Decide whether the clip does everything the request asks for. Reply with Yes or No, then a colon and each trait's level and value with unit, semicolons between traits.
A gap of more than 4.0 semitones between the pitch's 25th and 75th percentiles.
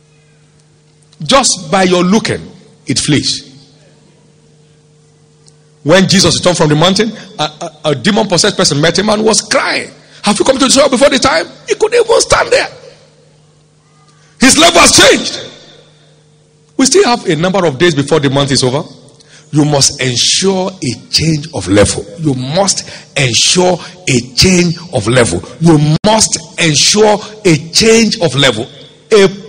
Yes: average, 4.6 semitones